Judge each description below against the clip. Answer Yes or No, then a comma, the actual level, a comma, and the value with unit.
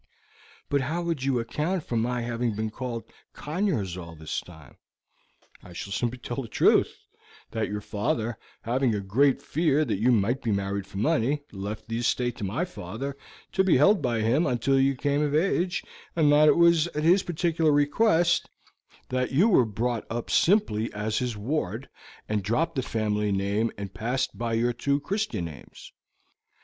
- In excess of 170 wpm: Yes, average, 180 wpm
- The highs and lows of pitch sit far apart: Yes, wide, 5.8 semitones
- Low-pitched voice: Yes, low, 125 Hz